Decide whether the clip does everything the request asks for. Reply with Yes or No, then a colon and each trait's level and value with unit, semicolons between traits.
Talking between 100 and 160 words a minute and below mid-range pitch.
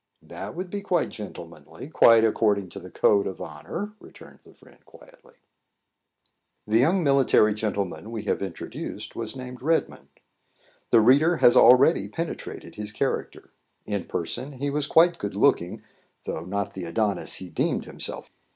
Yes: average, 150 wpm; low, 110 Hz